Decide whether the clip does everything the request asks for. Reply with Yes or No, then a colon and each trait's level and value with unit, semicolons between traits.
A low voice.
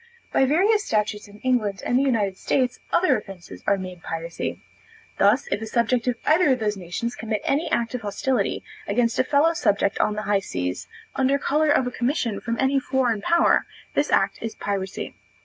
No: high, 230 Hz